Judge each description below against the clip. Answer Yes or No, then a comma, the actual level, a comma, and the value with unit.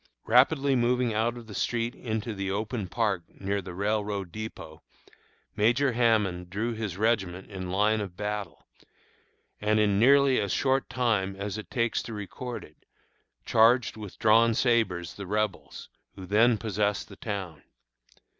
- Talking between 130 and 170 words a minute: Yes, average, 150 wpm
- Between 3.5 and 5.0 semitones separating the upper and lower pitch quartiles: No, average, 3.1 semitones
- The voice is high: No, low, 105 Hz